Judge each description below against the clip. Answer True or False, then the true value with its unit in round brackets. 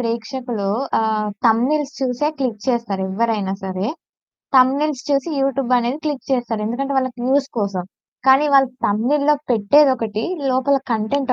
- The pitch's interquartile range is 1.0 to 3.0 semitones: False (3.9 semitones)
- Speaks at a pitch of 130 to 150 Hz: False (250 Hz)